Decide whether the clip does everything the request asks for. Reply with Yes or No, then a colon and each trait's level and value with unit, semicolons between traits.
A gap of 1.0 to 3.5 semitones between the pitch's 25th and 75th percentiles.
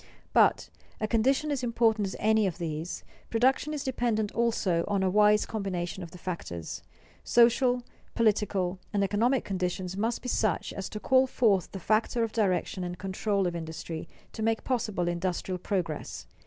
No: average, 4.2 semitones